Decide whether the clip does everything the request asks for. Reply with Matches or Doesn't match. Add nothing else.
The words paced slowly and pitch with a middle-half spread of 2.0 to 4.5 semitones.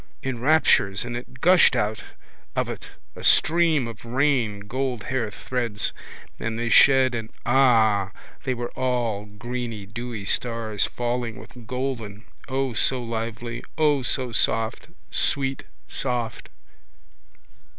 Matches